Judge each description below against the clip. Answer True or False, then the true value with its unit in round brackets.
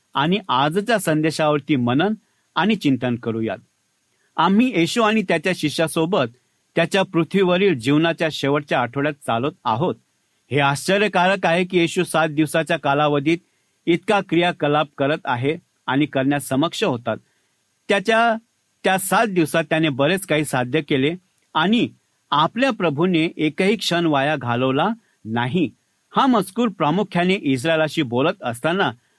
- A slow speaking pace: True (120 wpm)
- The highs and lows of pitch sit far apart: False (4.6 semitones)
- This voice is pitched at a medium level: True (165 Hz)